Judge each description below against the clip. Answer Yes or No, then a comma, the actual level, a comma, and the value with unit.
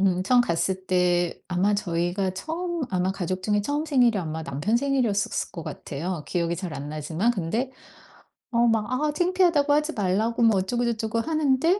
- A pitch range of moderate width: No, wide, 6.3 semitones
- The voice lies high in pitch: Yes, high, 210 Hz